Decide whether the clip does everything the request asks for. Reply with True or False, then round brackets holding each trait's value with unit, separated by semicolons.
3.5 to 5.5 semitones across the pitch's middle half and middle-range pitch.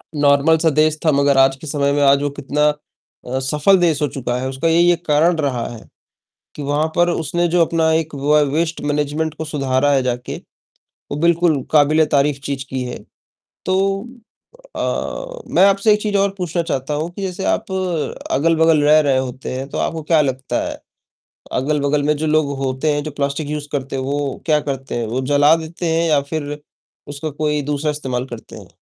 False (2.7 semitones; 150 Hz)